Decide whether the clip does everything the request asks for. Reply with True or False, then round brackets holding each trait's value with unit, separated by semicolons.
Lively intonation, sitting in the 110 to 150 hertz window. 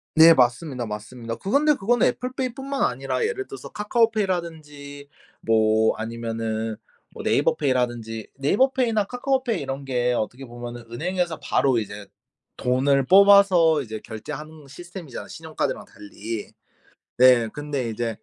True (8.2 semitones; 140 Hz)